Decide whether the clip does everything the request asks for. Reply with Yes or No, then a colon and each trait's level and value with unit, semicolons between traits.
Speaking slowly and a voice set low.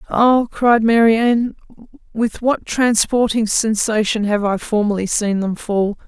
No: slow, 130 wpm; high, 220 Hz